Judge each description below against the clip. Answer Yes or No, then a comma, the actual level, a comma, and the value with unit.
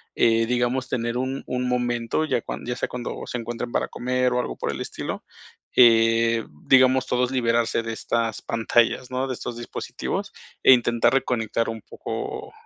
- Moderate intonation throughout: No, narrow, 1.5 semitones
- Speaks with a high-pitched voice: No, low, 120 Hz